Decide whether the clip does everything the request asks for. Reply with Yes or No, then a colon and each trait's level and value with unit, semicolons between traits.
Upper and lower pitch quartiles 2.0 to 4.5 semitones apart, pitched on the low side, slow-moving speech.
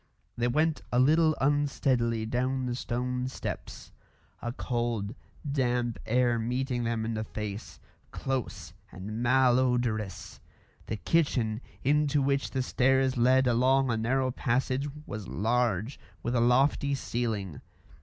Yes: narrow, 2.4 semitones; low, 125 Hz; slow, 130 wpm